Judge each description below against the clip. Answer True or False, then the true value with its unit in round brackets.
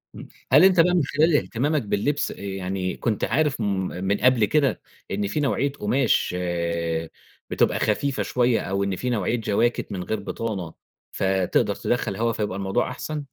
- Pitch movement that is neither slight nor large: False (6.2 semitones)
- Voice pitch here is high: False (115 Hz)